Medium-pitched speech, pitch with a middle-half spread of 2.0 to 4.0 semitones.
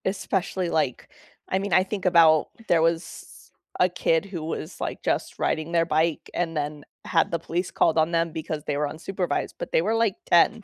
Yes: medium, 165 Hz; average, 2.7 semitones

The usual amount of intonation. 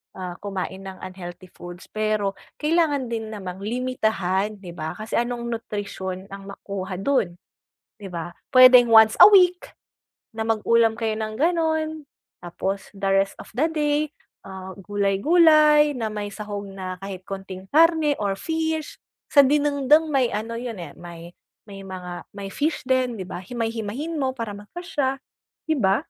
No: wide, 6.3 semitones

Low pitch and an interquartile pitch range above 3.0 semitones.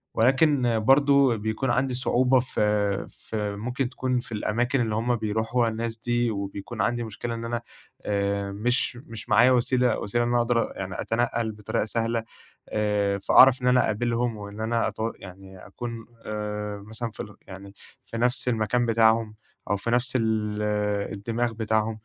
No: low, 115 Hz; narrow, 2.4 semitones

